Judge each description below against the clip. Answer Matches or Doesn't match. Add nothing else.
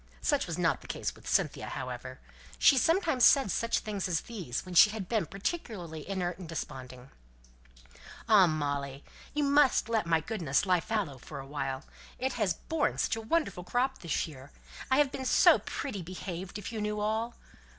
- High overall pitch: Matches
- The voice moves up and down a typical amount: Doesn't match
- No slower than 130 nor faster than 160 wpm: Doesn't match